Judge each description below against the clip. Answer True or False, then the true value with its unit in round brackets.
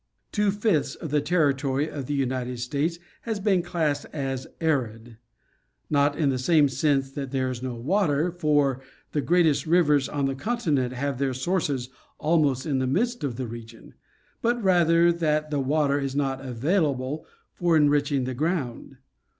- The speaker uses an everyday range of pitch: True (3.8 semitones)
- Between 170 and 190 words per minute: False (160 wpm)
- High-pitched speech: False (145 Hz)